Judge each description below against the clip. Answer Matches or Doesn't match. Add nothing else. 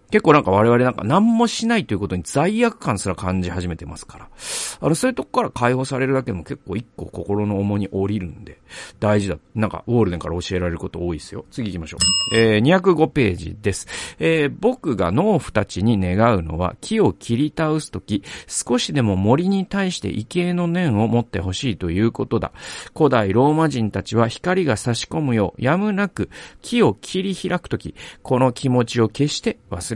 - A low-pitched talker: Matches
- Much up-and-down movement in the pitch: Matches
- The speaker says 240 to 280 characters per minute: Doesn't match